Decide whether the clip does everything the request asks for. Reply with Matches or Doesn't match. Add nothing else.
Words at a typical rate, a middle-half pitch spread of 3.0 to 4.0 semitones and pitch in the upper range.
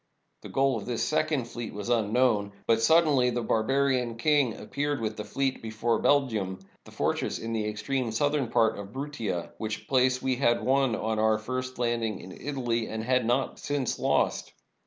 Doesn't match